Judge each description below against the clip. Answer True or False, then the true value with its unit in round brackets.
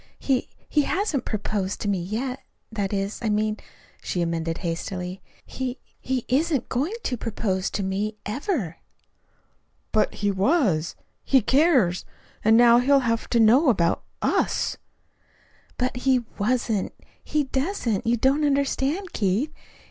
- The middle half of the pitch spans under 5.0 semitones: False (5.3 semitones)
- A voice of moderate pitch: False (230 Hz)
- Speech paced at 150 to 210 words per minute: False (135 wpm)